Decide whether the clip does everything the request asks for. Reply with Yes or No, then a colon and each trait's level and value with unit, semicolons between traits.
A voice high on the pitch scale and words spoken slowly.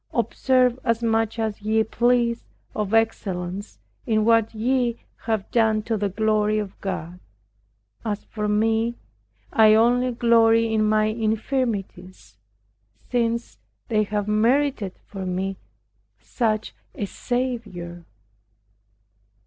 Yes: high, 220 Hz; slow, 110 wpm